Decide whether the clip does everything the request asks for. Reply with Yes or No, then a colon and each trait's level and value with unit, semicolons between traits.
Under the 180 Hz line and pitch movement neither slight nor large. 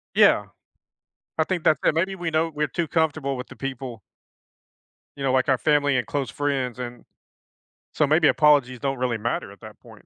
Yes: medium, 140 Hz; average, 3.6 semitones